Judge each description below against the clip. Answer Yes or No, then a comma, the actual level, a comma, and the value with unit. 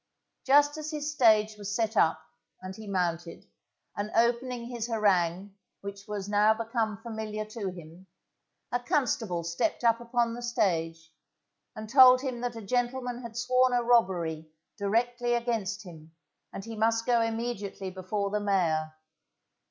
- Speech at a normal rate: Yes, average, 150 wpm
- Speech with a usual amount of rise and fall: Yes, average, 3.9 semitones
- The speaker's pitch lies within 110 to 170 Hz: No, high, 220 Hz